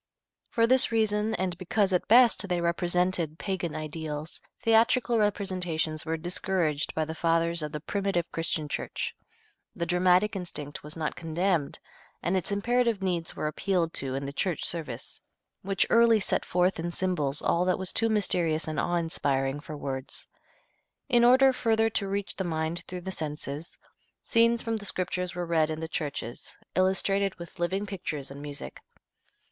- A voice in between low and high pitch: Yes, medium, 175 Hz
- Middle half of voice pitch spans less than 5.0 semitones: Yes, average, 4.1 semitones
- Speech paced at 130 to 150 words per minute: No, average, 165 wpm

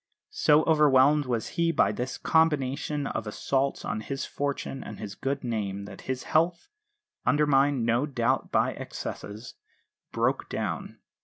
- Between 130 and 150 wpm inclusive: Yes, average, 140 wpm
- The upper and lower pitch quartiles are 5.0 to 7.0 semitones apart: No, average, 4.2 semitones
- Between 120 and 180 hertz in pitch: Yes, low, 135 Hz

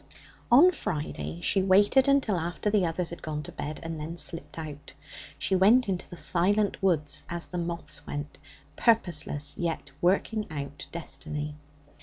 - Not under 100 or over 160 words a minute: Yes, average, 155 wpm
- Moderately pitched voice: Yes, medium, 170 Hz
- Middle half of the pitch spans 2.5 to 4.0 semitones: No, average, 4.4 semitones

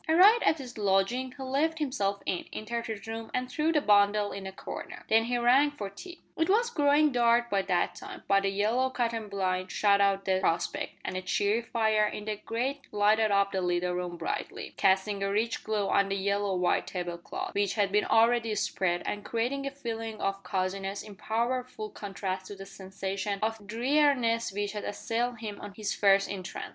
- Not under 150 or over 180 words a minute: No, average, 200 wpm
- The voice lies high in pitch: Yes, high, 210 Hz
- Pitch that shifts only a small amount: No, average, 3.4 semitones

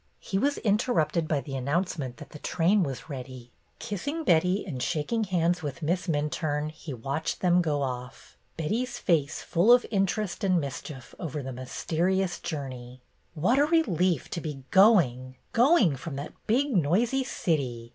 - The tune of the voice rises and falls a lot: Yes, wide, 5.8 semitones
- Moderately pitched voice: Yes, medium, 165 Hz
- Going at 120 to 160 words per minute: Yes, average, 155 wpm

